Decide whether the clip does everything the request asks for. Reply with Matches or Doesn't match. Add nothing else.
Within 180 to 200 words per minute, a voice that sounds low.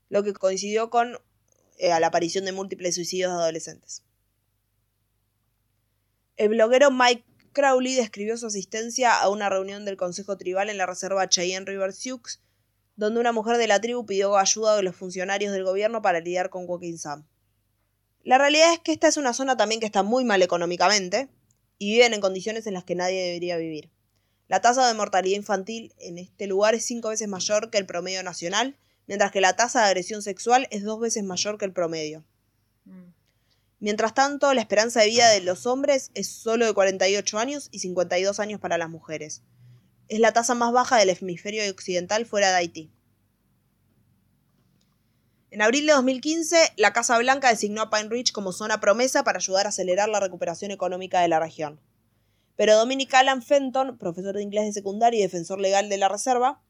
Doesn't match